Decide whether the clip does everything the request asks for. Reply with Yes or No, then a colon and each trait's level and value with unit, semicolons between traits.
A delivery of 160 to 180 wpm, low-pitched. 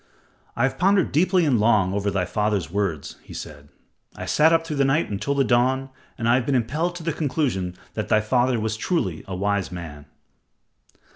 No: average, 200 wpm; low, 120 Hz